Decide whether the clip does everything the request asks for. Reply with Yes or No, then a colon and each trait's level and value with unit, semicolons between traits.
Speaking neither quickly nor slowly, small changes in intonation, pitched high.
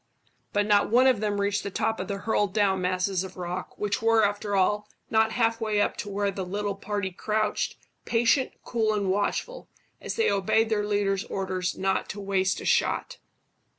Yes: average, 190 wpm; narrow, 2.1 semitones; high, 205 Hz